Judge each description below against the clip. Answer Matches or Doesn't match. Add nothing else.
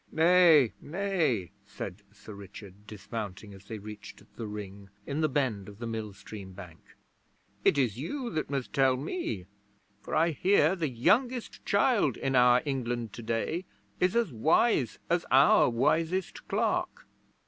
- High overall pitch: Doesn't match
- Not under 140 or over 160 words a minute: Matches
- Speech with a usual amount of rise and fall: Doesn't match